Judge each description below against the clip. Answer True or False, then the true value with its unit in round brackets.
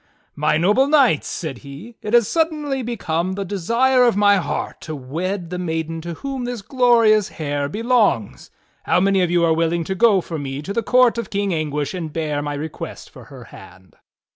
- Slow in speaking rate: False (200 wpm)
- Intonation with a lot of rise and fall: True (6.7 semitones)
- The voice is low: False (185 Hz)